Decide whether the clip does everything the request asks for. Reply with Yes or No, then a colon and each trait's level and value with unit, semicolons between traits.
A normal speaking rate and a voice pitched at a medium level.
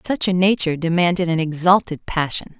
Yes: average, 160 wpm; medium, 175 Hz